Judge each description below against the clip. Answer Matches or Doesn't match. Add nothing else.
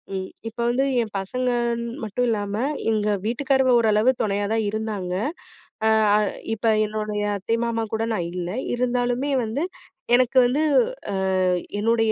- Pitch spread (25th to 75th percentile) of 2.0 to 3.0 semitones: Matches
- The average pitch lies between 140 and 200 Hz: Doesn't match